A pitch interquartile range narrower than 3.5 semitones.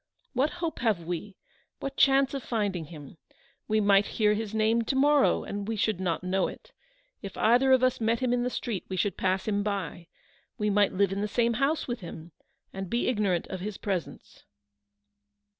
No: average, 4.1 semitones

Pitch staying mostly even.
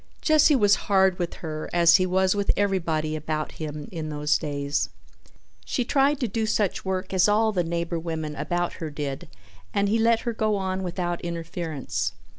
No: average, 4.4 semitones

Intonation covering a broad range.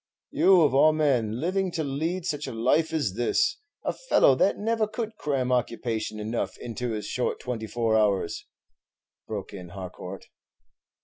Yes: wide, 6.8 semitones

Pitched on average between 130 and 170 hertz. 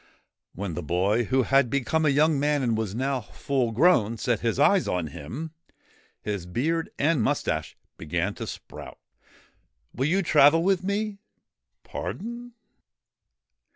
Yes: low, 135 Hz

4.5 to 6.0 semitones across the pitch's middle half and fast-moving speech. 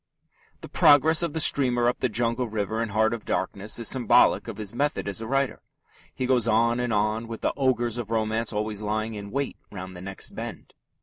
No: narrow, 2.5 semitones; fast, 210 wpm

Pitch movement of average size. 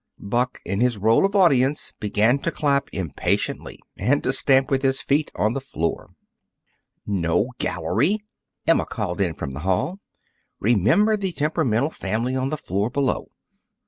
No: wide, 6.1 semitones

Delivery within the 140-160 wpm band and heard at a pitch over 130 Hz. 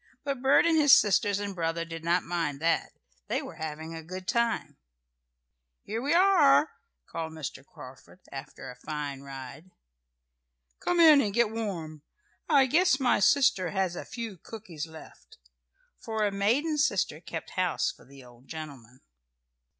Yes: average, 155 wpm; medium, 185 Hz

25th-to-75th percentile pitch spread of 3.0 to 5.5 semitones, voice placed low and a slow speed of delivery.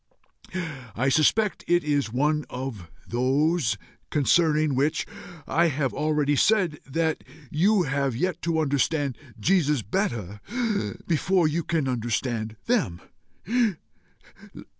No: average, 4.4 semitones; medium, 150 Hz; slow, 105 wpm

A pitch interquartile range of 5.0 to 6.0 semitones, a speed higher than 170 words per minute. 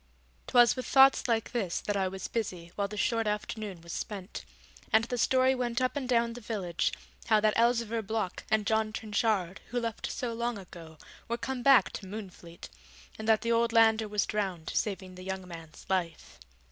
No: average, 3.5 semitones; average, 190 wpm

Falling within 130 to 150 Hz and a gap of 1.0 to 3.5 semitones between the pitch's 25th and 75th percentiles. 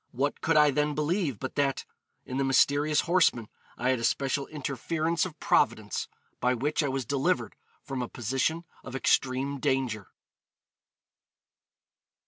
Yes: medium, 140 Hz; average, 2.7 semitones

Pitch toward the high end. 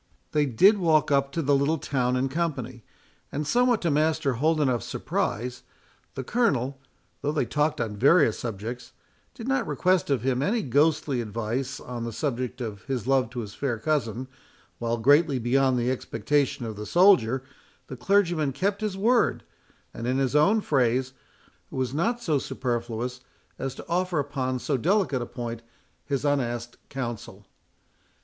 No: low, 135 Hz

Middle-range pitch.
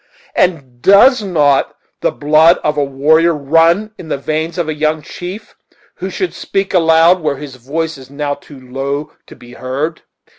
Yes: medium, 155 Hz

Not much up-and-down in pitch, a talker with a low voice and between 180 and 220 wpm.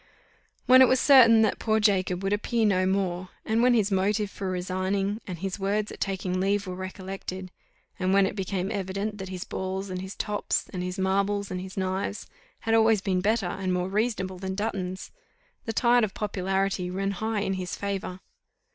No: narrow, 2.0 semitones; high, 195 Hz; average, 190 wpm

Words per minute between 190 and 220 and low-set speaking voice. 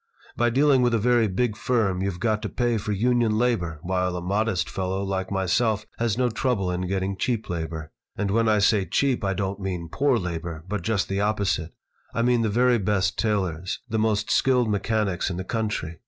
Yes: average, 200 wpm; low, 105 Hz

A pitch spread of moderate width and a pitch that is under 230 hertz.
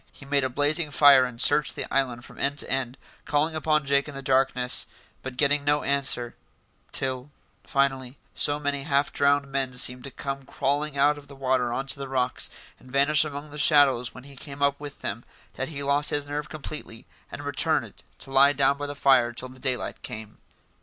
No: narrow, 1.7 semitones; medium, 140 Hz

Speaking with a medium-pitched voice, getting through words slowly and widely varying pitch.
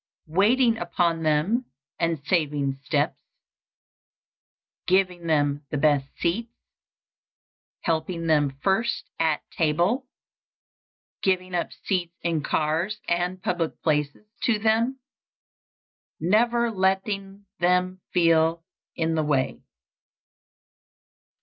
No: medium, 175 Hz; slow, 95 wpm; average, 3.6 semitones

